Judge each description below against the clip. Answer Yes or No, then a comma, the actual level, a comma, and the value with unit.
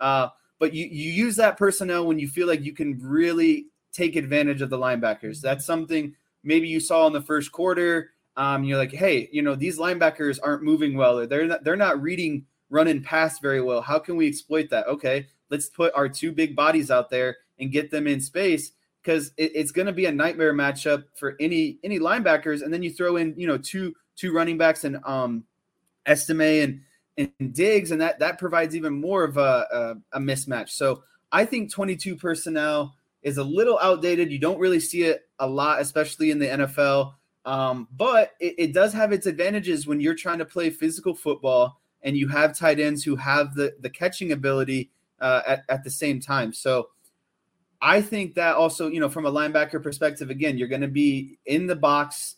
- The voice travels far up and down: No, average, 3.3 semitones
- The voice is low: No, medium, 155 Hz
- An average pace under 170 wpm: No, fast, 205 wpm